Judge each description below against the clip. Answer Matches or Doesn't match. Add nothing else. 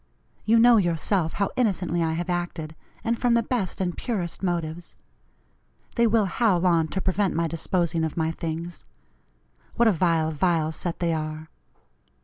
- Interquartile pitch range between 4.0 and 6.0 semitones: Doesn't match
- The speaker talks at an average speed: Matches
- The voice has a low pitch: Doesn't match